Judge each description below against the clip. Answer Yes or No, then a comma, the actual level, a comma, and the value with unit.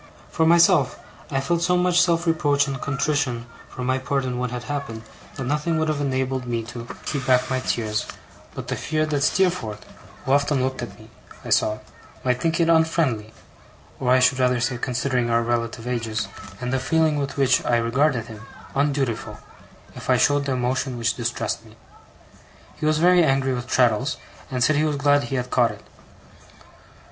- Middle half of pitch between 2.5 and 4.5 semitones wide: Yes, average, 3.4 semitones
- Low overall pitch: Yes, low, 130 Hz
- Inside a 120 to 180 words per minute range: No, average, 190 wpm